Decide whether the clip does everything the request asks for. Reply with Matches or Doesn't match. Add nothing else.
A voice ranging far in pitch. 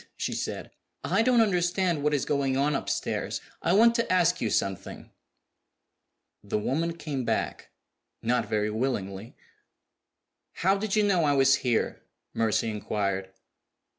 Matches